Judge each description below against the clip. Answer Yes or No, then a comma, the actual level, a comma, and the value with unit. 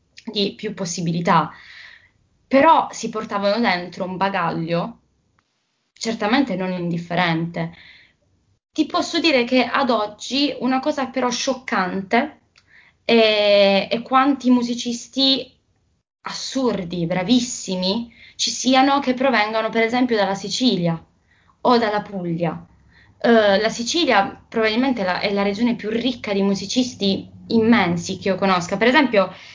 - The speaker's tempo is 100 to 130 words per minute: Yes, average, 120 wpm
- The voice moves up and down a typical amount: Yes, average, 4.7 semitones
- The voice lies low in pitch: No, high, 220 Hz